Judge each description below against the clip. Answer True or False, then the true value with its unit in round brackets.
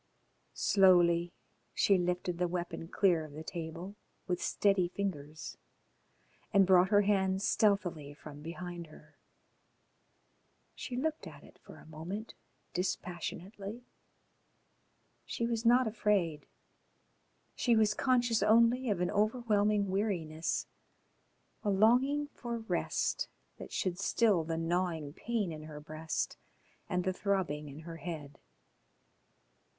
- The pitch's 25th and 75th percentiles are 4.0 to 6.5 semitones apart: True (4.3 semitones)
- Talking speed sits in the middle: False (120 wpm)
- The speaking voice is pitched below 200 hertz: True (185 Hz)